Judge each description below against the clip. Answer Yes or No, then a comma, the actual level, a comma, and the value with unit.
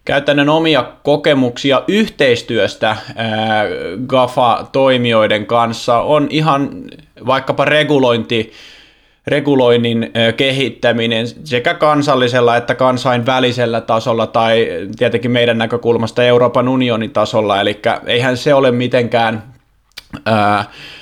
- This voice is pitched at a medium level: No, low, 120 Hz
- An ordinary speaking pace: No, slow, 90 wpm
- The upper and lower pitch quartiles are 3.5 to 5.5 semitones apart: No, average, 2.9 semitones